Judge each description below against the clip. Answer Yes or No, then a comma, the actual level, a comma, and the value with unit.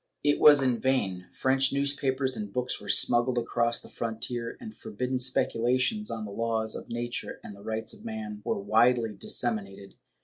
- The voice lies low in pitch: Yes, low, 120 Hz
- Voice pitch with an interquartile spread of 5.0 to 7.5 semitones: No, average, 3.2 semitones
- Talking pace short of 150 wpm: No, average, 175 wpm